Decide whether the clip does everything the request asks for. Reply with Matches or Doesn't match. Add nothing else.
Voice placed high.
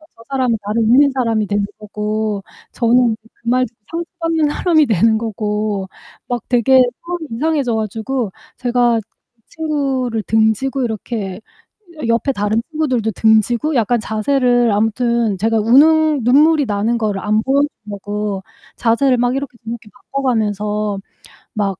Matches